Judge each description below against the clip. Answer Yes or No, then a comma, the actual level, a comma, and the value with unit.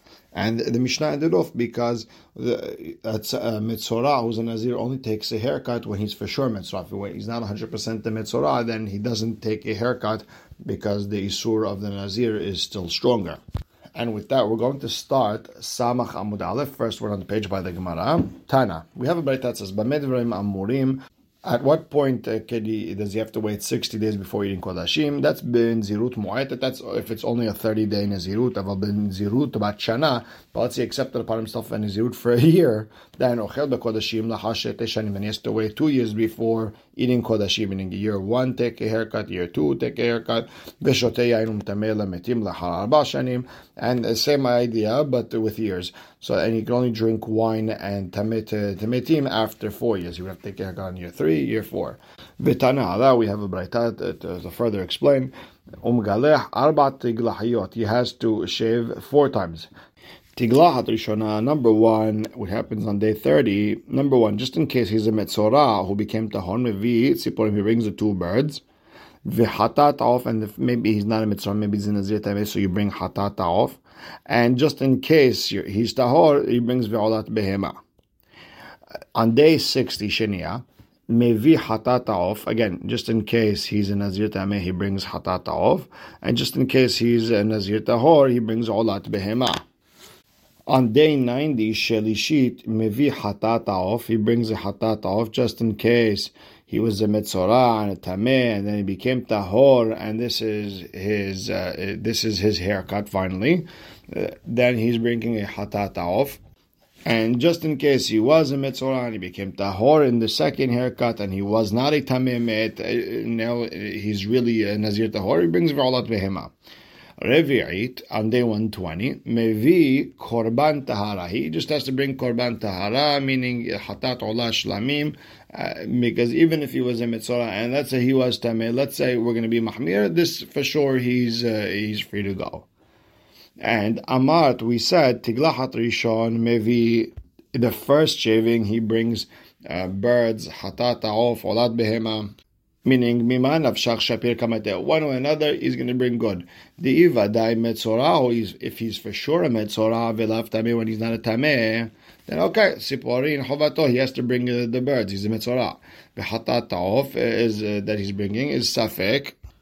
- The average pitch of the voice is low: Yes, low, 115 Hz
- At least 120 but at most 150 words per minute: No, average, 175 wpm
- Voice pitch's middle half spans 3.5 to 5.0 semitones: No, narrow, 2.6 semitones